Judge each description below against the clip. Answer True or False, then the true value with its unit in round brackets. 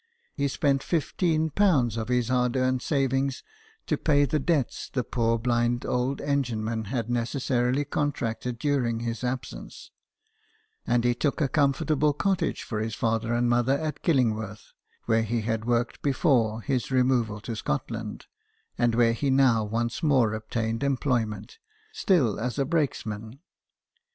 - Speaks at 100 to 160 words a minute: True (150 wpm)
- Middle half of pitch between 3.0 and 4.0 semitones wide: True (3.4 semitones)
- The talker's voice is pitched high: False (125 Hz)